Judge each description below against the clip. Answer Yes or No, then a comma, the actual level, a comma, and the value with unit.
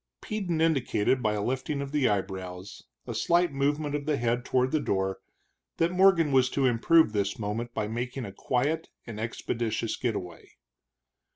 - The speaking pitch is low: Yes, low, 125 Hz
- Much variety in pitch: Yes, wide, 5.7 semitones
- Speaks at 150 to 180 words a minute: Yes, average, 170 wpm